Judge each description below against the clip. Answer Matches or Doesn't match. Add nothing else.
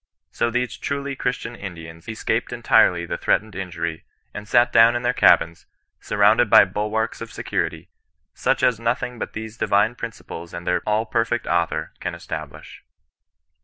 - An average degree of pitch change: Matches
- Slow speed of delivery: Doesn't match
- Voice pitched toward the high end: Doesn't match